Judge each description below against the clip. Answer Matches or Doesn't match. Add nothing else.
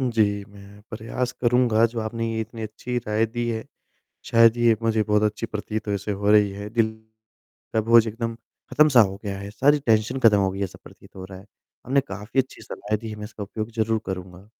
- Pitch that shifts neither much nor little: Doesn't match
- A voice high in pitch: Doesn't match